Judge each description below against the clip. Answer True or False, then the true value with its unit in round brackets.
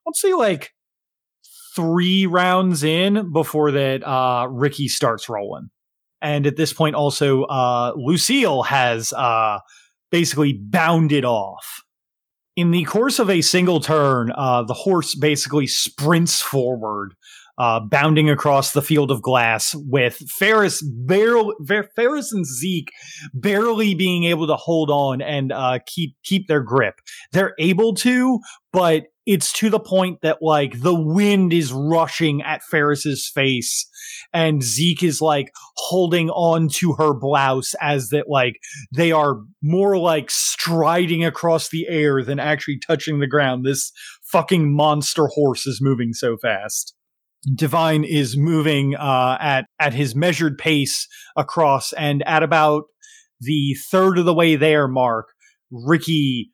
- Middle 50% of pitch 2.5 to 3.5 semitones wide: False (4.0 semitones)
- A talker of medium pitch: True (155 Hz)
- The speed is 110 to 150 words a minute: True (140 wpm)